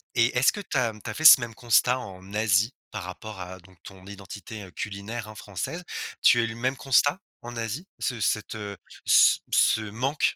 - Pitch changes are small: No, average, 3.7 semitones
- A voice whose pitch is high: No, low, 110 Hz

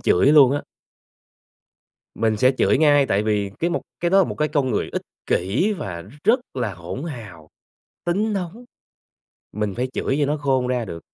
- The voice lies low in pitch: Yes, low, 130 Hz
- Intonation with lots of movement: Yes, wide, 6.9 semitones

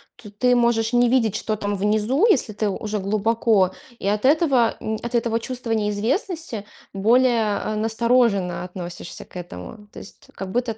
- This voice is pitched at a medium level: No, high, 220 Hz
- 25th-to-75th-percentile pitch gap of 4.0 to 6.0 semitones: No, average, 2.9 semitones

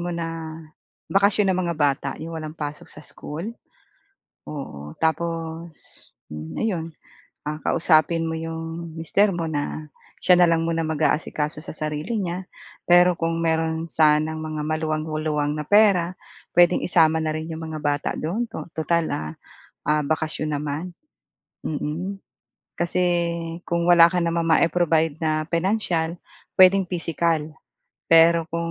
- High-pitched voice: No, medium, 165 Hz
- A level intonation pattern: Yes, narrow, 1.7 semitones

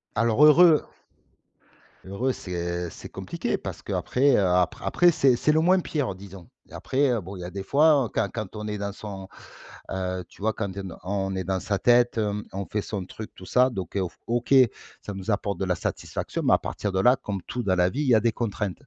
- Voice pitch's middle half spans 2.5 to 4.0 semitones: No, average, 4.6 semitones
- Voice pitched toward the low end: Yes, low, 105 Hz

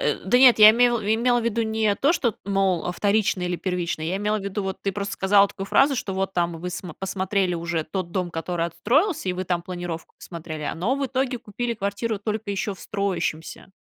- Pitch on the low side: No, high, 195 Hz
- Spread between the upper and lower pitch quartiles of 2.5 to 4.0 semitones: Yes, average, 3.7 semitones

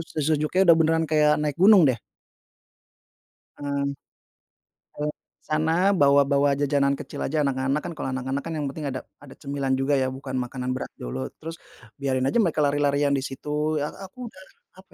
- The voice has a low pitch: No, medium, 145 Hz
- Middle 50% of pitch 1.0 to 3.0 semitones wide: Yes, narrow, 2.5 semitones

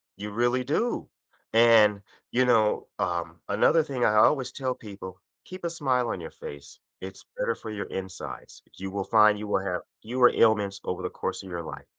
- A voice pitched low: Yes, low, 110 Hz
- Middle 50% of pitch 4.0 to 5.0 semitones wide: Yes, average, 4.4 semitones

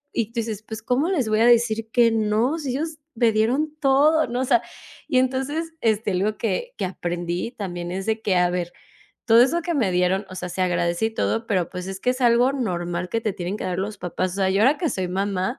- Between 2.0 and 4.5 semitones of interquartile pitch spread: No, average, 5.2 semitones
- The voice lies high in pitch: Yes, high, 220 Hz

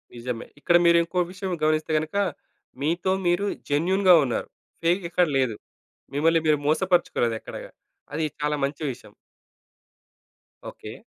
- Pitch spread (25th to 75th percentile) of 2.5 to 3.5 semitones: Yes, average, 3.2 semitones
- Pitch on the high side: No, medium, 165 Hz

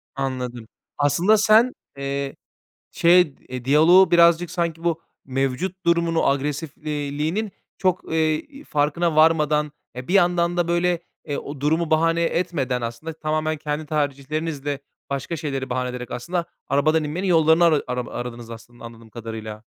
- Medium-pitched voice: Yes, medium, 155 Hz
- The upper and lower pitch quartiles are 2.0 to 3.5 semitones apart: No, average, 3.9 semitones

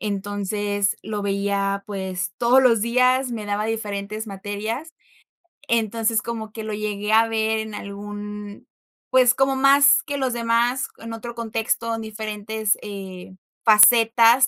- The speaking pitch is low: No, high, 220 Hz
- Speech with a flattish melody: Yes, narrow, 2.3 semitones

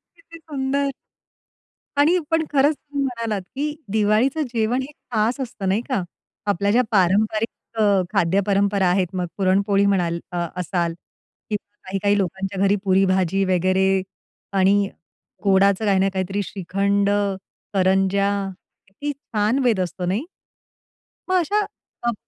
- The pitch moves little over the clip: No, average, 3.8 semitones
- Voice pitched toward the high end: Yes, high, 200 Hz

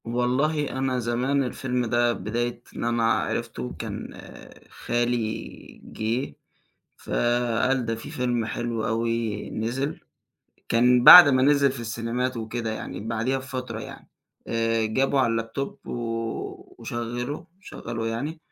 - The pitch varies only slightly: Yes, narrow, 2.2 semitones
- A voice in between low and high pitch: No, low, 120 Hz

